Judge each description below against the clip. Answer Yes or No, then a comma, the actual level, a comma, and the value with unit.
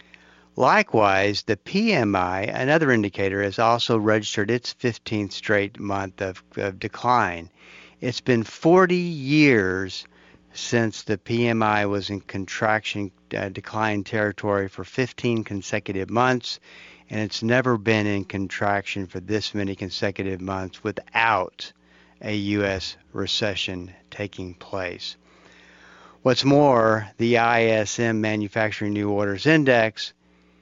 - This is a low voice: Yes, low, 105 Hz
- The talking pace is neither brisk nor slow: No, slow, 110 wpm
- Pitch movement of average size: Yes, average, 3.1 semitones